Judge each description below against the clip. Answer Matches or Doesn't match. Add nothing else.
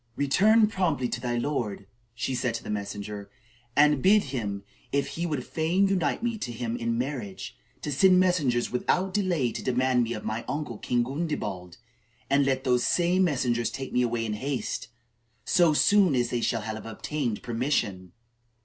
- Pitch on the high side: Doesn't match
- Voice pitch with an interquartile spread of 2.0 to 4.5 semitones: Doesn't match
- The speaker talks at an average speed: Matches